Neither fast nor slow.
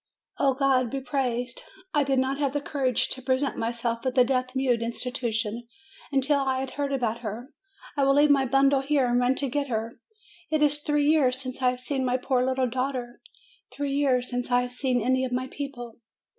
No: fast, 210 wpm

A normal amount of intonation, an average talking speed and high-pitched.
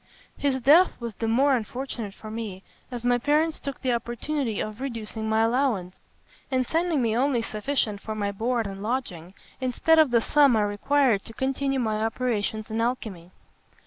Yes: average, 3.8 semitones; average, 175 wpm; high, 235 Hz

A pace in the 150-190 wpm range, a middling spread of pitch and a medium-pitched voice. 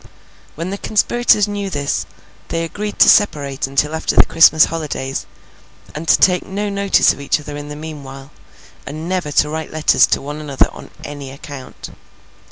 Yes: average, 175 wpm; average, 4.5 semitones; medium, 155 Hz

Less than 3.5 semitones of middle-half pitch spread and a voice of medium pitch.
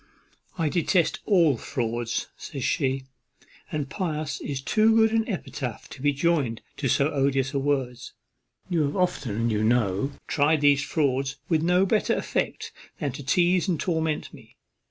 No: average, 4.4 semitones; medium, 145 Hz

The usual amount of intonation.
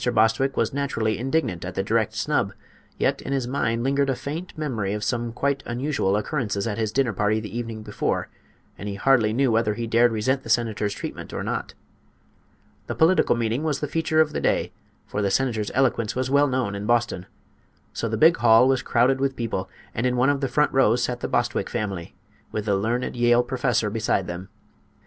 Yes: average, 3.8 semitones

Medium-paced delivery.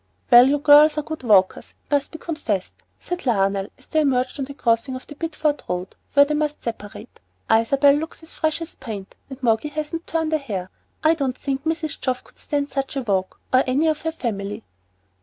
No: fast, 210 wpm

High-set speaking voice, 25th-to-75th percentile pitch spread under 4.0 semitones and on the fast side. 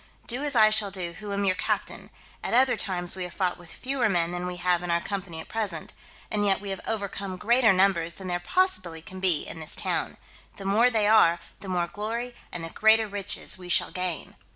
Yes: high, 195 Hz; average, 3.4 semitones; fast, 225 wpm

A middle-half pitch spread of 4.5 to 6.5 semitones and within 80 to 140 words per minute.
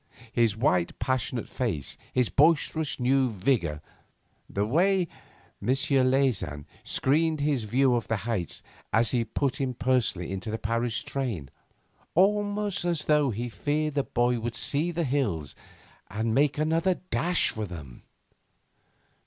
Yes: average, 5.2 semitones; slow, 135 wpm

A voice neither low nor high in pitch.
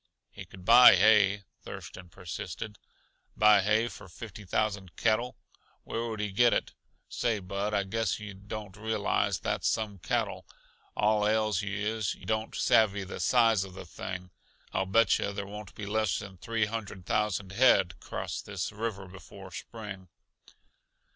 No: low, 105 Hz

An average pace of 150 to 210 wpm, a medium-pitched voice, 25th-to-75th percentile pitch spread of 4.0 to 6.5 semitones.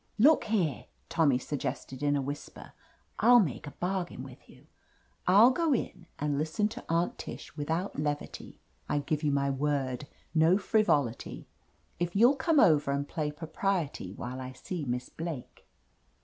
Yes: average, 165 wpm; medium, 150 Hz; average, 5.2 semitones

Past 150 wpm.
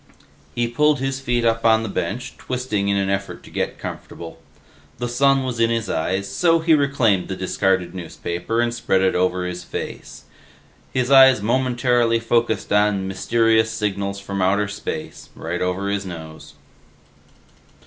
Yes: average, 160 wpm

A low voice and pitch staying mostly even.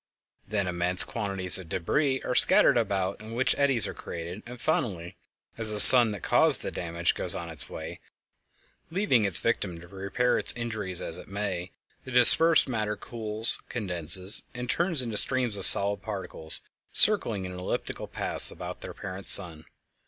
No: low, 100 Hz; average, 4.9 semitones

